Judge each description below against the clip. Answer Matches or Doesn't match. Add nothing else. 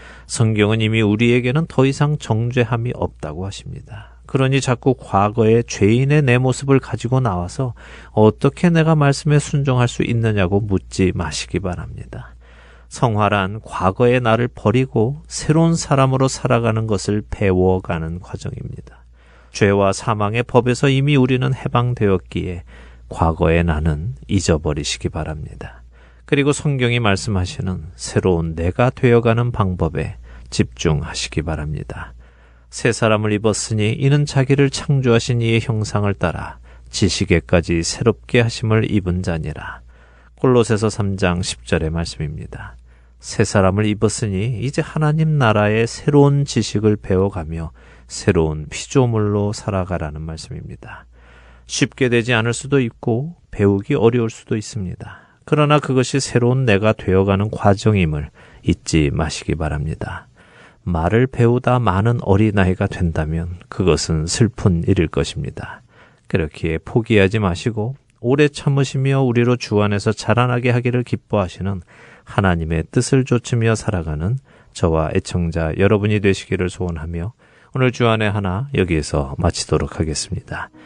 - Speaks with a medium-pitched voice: Doesn't match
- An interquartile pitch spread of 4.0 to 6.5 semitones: Matches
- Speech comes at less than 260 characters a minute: Doesn't match